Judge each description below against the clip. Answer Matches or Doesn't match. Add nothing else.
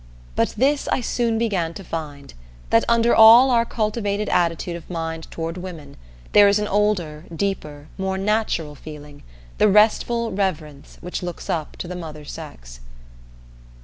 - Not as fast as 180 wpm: Matches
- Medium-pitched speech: Matches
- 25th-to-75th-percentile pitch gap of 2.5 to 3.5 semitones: Doesn't match